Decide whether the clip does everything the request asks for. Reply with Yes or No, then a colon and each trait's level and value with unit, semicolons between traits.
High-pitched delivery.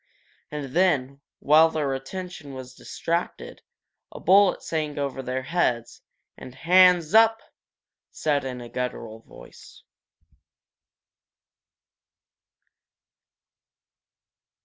No: medium, 145 Hz